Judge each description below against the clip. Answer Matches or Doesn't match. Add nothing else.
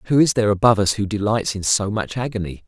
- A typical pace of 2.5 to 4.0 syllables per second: Doesn't match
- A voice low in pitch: Matches